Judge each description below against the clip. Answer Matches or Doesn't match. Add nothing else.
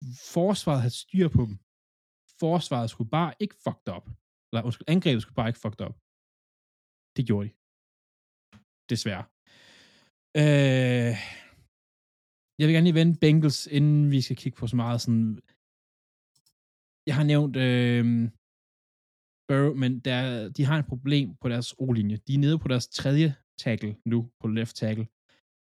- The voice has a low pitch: Matches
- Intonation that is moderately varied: Matches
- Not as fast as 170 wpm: Matches